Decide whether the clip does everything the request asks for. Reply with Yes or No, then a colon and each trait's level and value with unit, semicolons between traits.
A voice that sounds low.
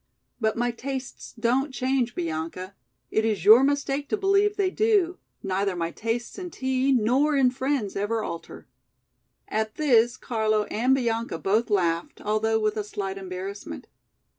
No: high, 230 Hz